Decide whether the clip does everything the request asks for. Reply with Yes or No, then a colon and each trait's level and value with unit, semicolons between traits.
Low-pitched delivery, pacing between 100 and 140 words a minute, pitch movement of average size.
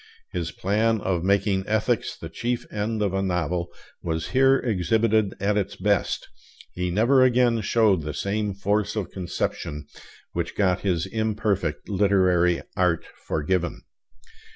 Yes: low, 100 Hz; slow, 135 wpm; average, 3.5 semitones